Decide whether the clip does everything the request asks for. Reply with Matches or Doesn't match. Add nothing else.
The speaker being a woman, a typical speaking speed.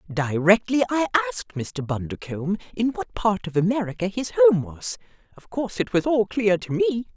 Matches